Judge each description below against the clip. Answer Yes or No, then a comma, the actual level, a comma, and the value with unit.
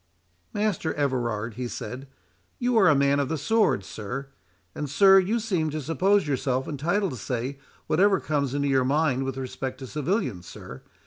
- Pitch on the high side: No, medium, 140 Hz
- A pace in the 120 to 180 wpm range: Yes, average, 175 wpm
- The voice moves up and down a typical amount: No, wide, 5.7 semitones